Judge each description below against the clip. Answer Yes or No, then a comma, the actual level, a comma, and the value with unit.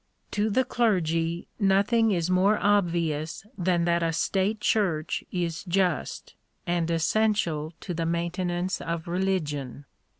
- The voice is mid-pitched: Yes, medium, 175 Hz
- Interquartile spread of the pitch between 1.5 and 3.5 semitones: Yes, average, 3.0 semitones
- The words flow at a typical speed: No, slow, 125 wpm